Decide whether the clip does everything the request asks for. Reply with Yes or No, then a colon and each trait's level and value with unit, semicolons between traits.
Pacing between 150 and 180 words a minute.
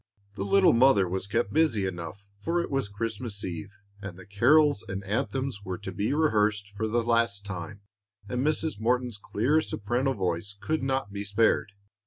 Yes: average, 175 wpm